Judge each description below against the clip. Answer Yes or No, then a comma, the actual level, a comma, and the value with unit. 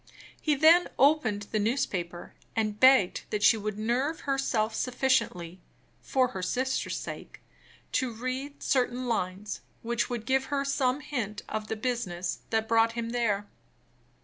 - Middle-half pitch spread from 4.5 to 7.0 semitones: No, average, 3.9 semitones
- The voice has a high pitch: Yes, high, 235 Hz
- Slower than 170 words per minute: Yes, average, 145 wpm